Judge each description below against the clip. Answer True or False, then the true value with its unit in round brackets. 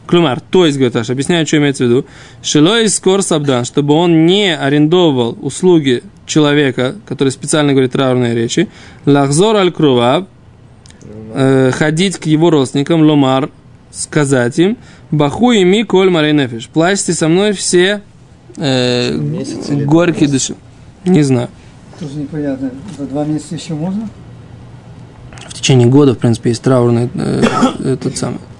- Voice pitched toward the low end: False (145 Hz)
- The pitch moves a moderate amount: True (4.5 semitones)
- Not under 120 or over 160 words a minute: True (125 wpm)